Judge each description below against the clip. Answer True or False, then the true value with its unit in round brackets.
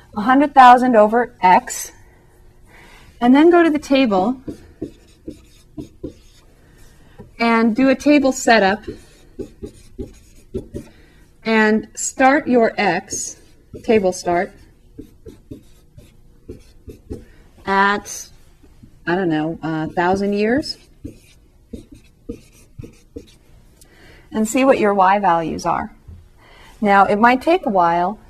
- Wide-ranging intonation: True (5.9 semitones)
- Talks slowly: True (85 wpm)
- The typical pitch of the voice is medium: False (220 Hz)